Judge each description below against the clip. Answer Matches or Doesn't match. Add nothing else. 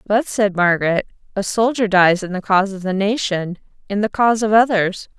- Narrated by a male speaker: Doesn't match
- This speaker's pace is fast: Doesn't match